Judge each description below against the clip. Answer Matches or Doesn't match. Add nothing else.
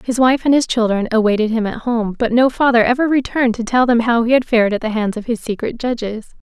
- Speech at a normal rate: Doesn't match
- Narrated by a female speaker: Matches